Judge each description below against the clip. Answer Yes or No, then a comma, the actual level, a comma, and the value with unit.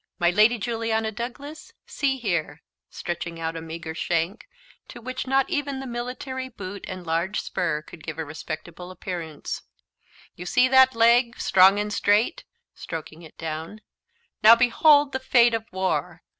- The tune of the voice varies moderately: No, wide, 6.4 semitones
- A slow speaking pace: No, average, 155 wpm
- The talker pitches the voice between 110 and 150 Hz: No, high, 210 Hz